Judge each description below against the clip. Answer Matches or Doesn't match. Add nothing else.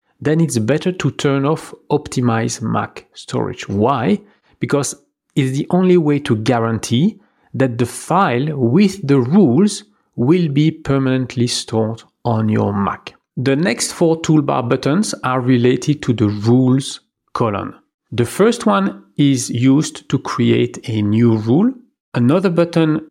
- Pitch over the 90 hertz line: Matches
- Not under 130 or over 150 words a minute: Matches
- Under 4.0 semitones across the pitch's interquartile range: Doesn't match